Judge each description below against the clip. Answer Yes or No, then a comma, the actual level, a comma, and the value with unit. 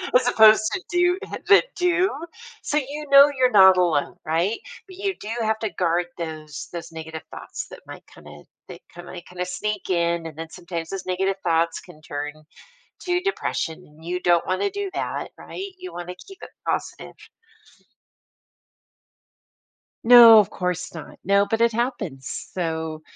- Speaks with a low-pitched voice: No, medium, 185 Hz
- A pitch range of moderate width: No, wide, 7.1 semitones